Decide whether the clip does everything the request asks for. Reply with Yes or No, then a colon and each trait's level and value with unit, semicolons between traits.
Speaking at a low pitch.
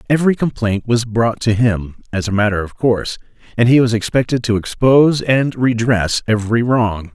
Yes: low, 115 Hz